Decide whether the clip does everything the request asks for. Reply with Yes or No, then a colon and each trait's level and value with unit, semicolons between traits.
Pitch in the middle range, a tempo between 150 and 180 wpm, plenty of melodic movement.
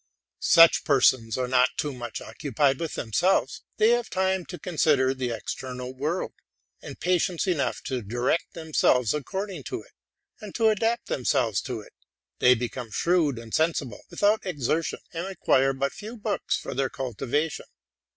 Yes: medium, 145 Hz; average, 155 wpm; wide, 6.2 semitones